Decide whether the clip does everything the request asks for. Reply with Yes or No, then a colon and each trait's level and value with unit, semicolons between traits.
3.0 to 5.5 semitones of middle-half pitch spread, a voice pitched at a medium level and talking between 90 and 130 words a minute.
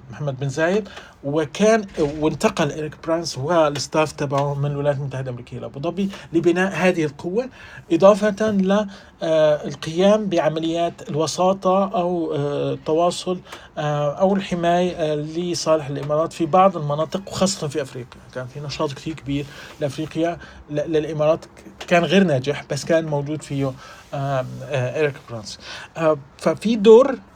Yes: average, 3.5 semitones; medium, 155 Hz; average, 115 wpm